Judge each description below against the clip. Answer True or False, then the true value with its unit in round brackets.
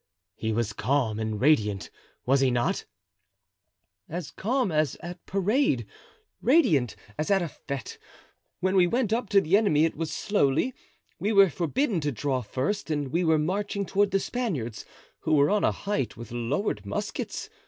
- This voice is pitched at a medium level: True (155 Hz)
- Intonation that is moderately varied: False (7.6 semitones)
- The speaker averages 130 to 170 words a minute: True (165 wpm)